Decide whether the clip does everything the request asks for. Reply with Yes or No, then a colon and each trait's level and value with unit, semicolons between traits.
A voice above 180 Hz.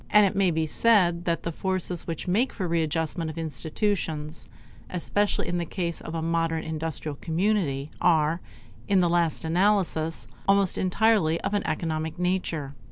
No: medium, 170 Hz